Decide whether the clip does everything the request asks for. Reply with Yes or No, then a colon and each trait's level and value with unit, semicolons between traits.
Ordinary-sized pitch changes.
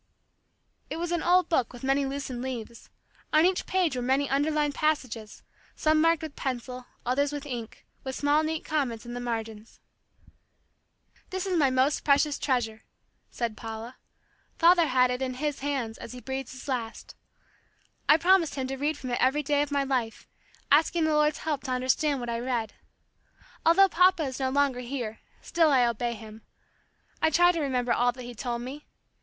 Yes: average, 3.8 semitones